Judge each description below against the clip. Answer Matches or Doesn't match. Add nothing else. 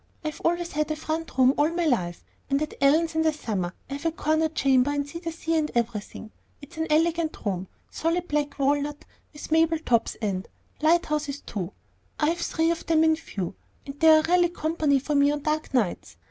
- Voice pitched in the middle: Doesn't match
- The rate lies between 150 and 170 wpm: Doesn't match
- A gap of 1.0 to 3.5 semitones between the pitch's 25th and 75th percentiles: Matches